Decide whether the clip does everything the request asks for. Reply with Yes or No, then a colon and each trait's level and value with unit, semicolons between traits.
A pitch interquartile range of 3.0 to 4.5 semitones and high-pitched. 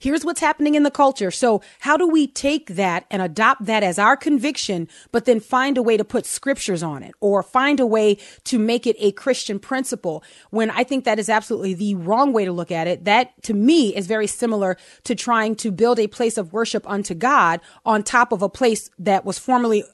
Yes: average, 4.2 semitones; high, 220 Hz